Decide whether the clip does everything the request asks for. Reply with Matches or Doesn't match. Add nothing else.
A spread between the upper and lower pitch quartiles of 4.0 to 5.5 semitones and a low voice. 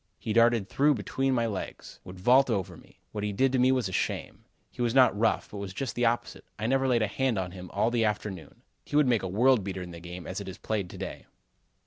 Matches